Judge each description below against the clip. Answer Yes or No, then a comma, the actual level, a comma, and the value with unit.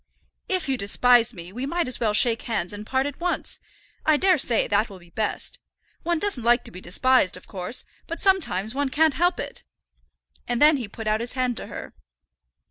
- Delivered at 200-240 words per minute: Yes, fast, 205 wpm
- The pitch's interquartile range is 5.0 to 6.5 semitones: Yes, wide, 5.6 semitones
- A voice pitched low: No, high, 245 Hz